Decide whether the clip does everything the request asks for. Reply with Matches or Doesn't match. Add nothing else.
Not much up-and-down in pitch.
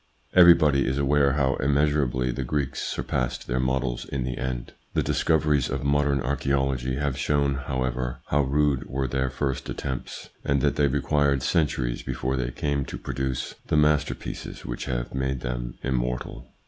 Matches